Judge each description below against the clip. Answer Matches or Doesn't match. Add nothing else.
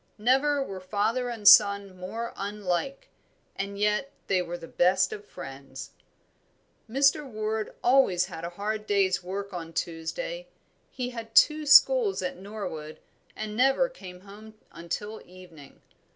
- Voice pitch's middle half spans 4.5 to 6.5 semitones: Matches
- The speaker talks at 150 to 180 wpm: Doesn't match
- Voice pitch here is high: Matches